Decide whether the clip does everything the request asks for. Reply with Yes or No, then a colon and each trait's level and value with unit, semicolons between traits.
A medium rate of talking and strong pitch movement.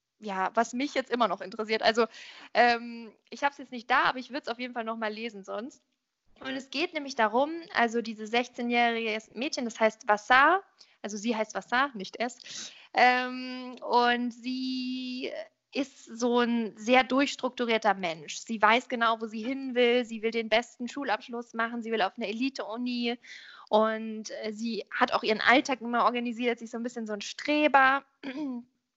No: average, 180 wpm; narrow, 2.5 semitones